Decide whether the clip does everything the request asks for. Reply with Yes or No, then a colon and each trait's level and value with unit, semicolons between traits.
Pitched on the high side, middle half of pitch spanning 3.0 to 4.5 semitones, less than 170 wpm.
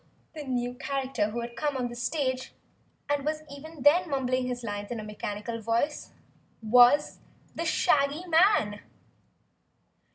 Yes: very high, 255 Hz; average, 3.8 semitones; average, 140 wpm